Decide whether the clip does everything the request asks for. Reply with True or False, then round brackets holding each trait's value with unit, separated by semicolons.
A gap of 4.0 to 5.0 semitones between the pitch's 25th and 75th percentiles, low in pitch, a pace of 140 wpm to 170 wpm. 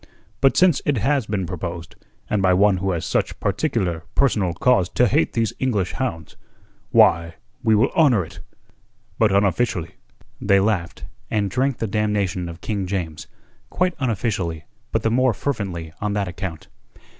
True (4.6 semitones; 100 Hz; 155 wpm)